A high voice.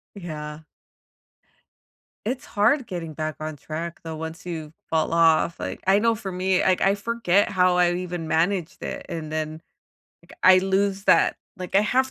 No: medium, 180 Hz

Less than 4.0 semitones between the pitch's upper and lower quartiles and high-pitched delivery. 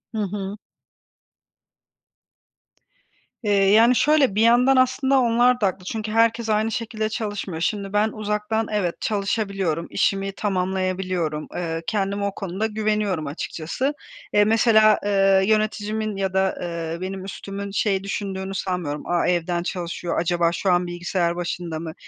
Yes: average, 3.3 semitones; high, 195 Hz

